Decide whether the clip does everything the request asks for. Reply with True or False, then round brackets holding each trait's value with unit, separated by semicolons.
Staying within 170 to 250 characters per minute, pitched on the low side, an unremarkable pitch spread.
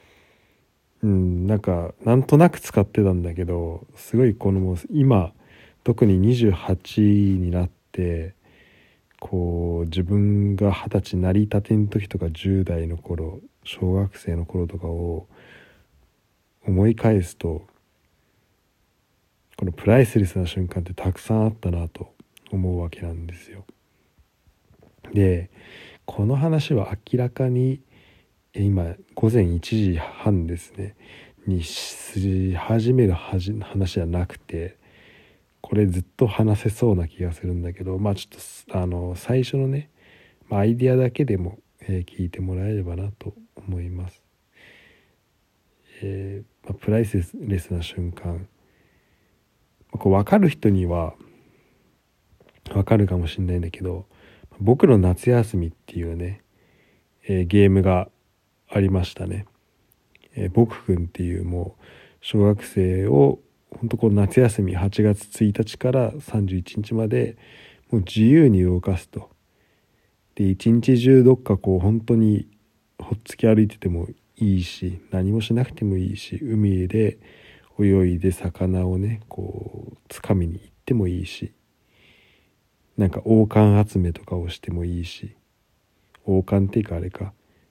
True (235 characters per minute; 100 Hz; 3.3 semitones)